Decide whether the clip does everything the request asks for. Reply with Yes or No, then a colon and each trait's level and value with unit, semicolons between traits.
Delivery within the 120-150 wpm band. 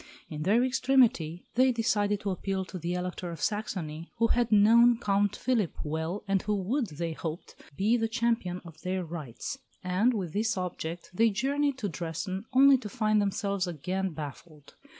No: average, 170 wpm